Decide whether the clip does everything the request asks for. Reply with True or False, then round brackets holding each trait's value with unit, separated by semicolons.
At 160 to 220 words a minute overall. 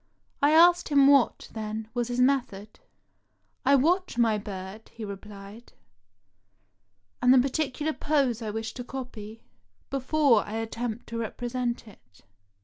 False (140 wpm)